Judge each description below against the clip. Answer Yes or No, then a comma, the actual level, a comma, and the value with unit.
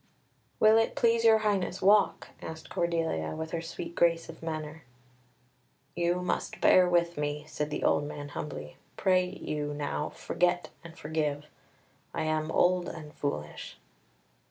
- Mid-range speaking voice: Yes, medium, 165 Hz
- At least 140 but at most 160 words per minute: Yes, average, 145 wpm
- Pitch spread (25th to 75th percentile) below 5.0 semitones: Yes, average, 3.2 semitones